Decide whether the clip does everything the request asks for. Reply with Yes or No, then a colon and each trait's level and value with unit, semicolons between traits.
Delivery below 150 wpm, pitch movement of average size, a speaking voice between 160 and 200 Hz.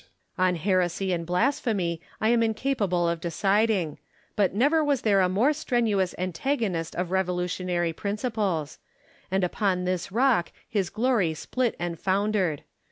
Yes: average, 140 wpm; average, 4.0 semitones; high, 190 Hz